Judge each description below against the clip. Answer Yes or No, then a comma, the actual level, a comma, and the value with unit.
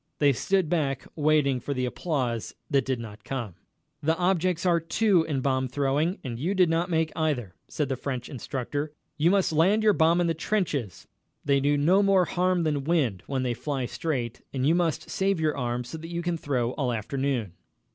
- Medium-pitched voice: Yes, medium, 150 Hz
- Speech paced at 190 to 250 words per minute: Yes, average, 200 wpm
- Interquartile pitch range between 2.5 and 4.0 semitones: No, average, 4.7 semitones